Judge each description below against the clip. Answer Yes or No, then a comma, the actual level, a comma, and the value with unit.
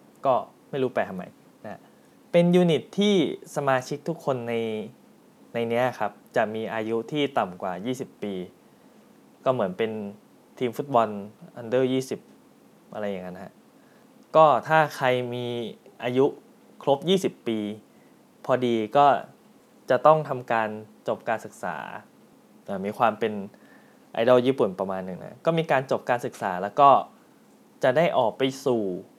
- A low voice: Yes, low, 125 Hz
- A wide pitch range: Yes, wide, 5.8 semitones